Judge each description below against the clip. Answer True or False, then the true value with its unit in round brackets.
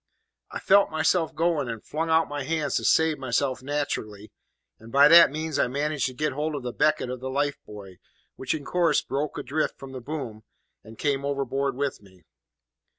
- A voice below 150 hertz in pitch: True (140 Hz)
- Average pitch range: True (3.4 semitones)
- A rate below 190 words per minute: False (195 wpm)